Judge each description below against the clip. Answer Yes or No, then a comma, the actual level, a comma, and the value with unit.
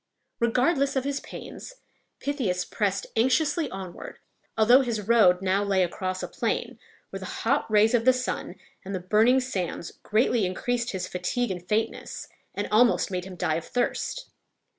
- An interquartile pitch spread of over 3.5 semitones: Yes, average, 5.1 semitones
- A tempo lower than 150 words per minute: No, average, 160 wpm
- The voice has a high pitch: Yes, high, 220 Hz